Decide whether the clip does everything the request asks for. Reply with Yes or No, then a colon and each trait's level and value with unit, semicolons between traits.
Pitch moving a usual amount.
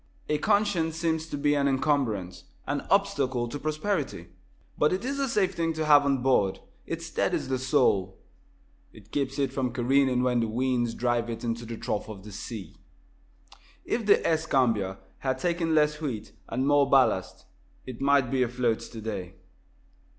Yes: average, 4.5 semitones